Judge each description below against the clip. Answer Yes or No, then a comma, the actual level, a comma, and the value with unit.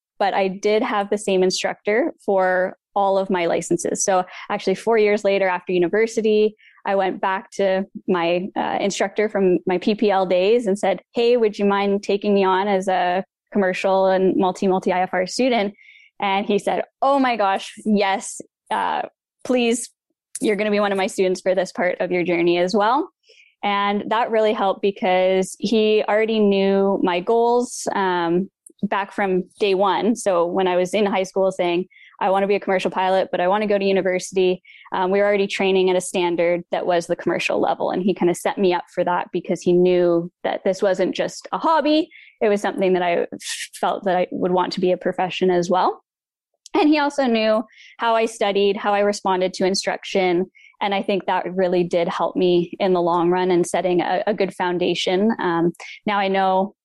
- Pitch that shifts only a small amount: Yes, narrow, 2.2 semitones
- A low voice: No, high, 195 Hz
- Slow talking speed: No, average, 200 wpm